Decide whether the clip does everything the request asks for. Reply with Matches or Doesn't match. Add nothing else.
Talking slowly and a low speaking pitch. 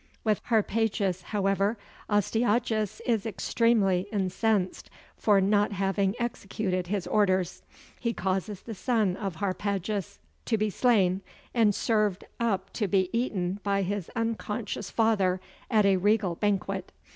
Doesn't match